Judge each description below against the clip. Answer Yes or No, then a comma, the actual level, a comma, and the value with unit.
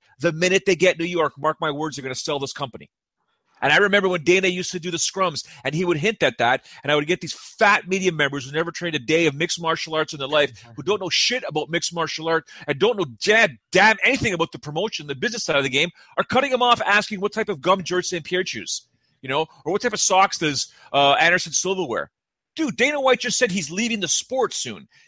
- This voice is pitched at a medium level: Yes, medium, 175 Hz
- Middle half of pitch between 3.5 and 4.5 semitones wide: Yes, average, 4.1 semitones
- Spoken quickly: Yes, fast, 260 wpm